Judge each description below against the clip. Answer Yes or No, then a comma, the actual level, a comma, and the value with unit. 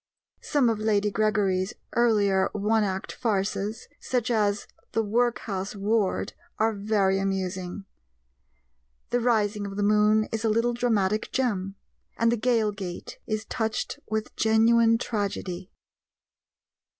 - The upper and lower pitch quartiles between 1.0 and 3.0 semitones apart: Yes, narrow, 2.4 semitones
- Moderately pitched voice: No, high, 215 Hz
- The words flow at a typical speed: No, slow, 125 wpm